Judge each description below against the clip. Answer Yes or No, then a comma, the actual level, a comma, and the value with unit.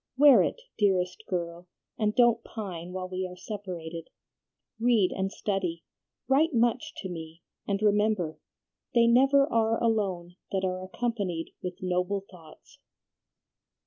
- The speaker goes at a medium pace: No, slow, 130 wpm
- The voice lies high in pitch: Yes, high, 195 Hz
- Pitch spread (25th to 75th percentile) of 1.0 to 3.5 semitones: No, average, 4.0 semitones